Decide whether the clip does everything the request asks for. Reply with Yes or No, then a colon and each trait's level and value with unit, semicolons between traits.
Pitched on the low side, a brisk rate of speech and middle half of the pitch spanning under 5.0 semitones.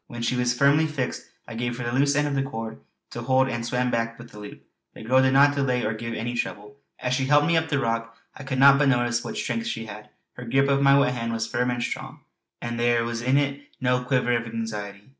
Yes: low, 125 Hz; fast, 260 wpm; average, 3.0 semitones